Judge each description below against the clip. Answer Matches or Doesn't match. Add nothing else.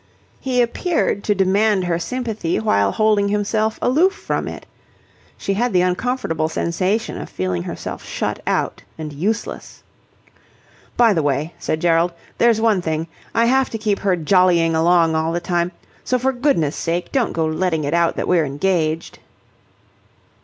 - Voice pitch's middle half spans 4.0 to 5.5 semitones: Matches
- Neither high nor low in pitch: Matches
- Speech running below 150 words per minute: Doesn't match